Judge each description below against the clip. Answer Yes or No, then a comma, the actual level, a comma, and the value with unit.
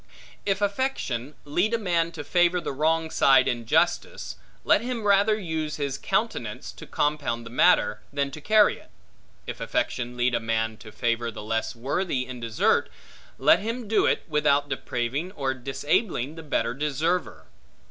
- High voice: No, medium, 145 Hz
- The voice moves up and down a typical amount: No, wide, 6.7 semitones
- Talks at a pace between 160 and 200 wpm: Yes, average, 165 wpm